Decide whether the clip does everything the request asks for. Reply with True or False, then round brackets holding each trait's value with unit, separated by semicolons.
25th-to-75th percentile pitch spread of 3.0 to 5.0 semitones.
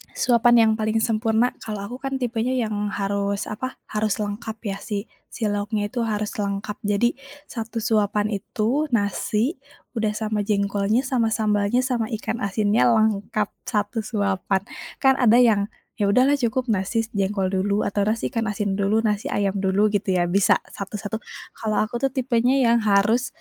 False (2.4 semitones)